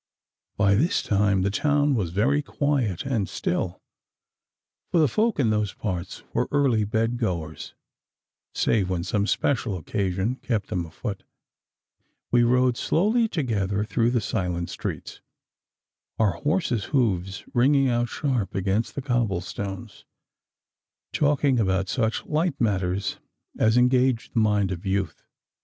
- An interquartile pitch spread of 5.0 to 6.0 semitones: Yes, average, 5.3 semitones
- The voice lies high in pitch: No, low, 110 Hz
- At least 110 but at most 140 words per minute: Yes, slow, 135 wpm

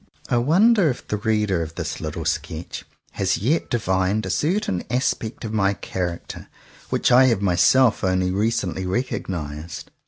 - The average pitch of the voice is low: Yes, low, 105 Hz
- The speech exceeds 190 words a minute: No, average, 150 wpm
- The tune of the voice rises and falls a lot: No, average, 4.9 semitones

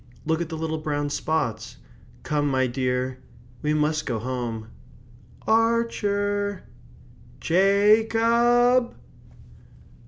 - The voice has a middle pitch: Yes, medium, 160 Hz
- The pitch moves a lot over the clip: Yes, wide, 8.2 semitones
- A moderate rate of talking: No, slow, 100 wpm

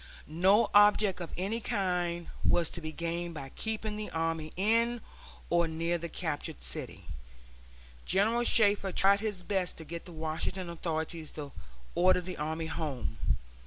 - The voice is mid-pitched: Yes, medium, 175 Hz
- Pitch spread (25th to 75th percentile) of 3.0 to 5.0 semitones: Yes, average, 3.8 semitones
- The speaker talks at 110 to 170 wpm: Yes, average, 150 wpm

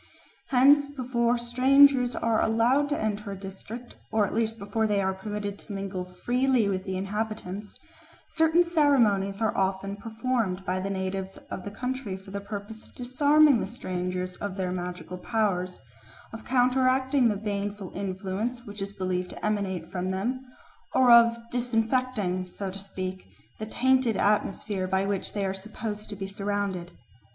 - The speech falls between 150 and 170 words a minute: Yes, average, 160 wpm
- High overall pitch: Yes, high, 205 Hz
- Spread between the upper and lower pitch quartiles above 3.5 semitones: Yes, average, 4.2 semitones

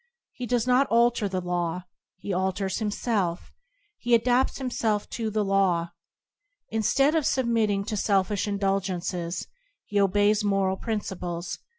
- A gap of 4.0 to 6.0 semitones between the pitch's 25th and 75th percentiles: No, average, 3.4 semitones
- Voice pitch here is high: Yes, high, 205 Hz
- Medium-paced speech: No, slow, 130 wpm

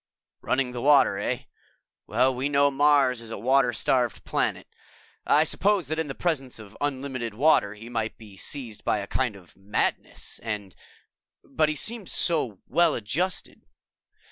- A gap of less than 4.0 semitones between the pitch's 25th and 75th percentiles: No, average, 4.8 semitones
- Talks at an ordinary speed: Yes, average, 155 wpm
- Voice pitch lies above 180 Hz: No, low, 130 Hz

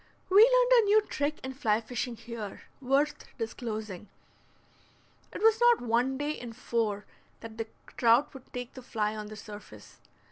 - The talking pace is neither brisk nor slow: Yes, average, 165 wpm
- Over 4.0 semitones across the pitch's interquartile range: Yes, average, 4.9 semitones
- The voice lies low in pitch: No, high, 240 Hz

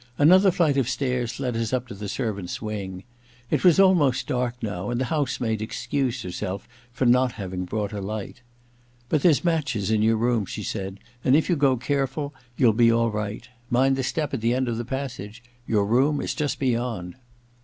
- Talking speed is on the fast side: Yes, fast, 210 wpm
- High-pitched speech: No, low, 120 Hz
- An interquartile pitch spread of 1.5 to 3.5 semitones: No, average, 3.9 semitones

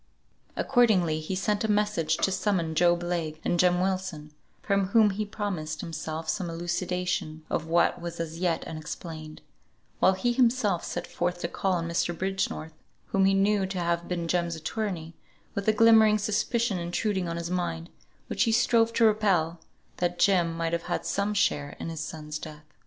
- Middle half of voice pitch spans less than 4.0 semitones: Yes, average, 3.4 semitones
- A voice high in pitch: No, medium, 175 Hz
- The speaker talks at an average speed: Yes, average, 175 wpm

